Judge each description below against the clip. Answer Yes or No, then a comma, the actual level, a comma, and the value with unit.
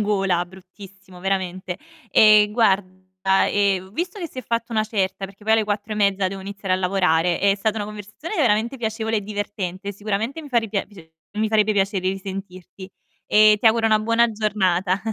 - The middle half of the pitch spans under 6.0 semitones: Yes, narrow, 2.4 semitones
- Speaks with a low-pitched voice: No, high, 205 Hz